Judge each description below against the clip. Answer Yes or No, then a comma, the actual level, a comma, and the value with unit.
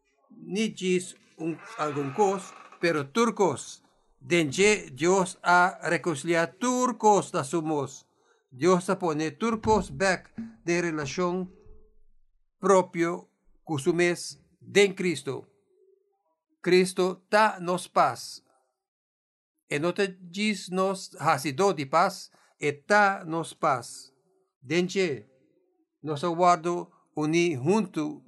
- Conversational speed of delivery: No, slow, 95 wpm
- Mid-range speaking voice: Yes, medium, 180 Hz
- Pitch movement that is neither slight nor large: Yes, average, 3.5 semitones